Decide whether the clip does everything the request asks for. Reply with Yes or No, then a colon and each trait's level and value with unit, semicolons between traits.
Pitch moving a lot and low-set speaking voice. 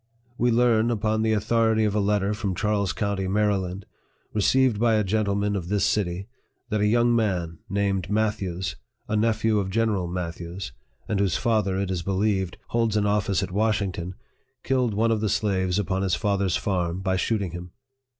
No: narrow, 2.6 semitones; low, 100 Hz